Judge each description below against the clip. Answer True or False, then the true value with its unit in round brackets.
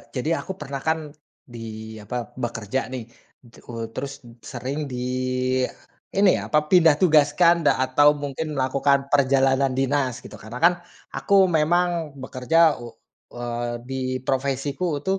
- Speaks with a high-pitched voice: False (135 Hz)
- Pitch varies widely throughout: False (2.9 semitones)